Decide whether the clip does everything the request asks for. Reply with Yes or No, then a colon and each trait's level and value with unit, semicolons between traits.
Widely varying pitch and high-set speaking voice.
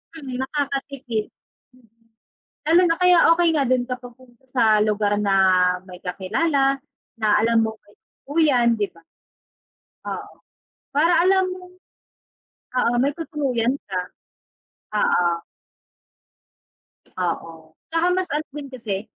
Yes: wide, 6.3 semitones; very high, 255 Hz